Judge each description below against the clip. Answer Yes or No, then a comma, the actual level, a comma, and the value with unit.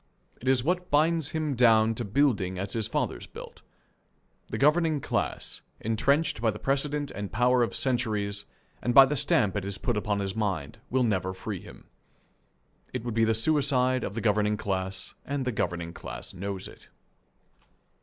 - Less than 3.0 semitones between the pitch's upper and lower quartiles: No, average, 5.1 semitones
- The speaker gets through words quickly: No, average, 175 wpm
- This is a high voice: No, low, 115 Hz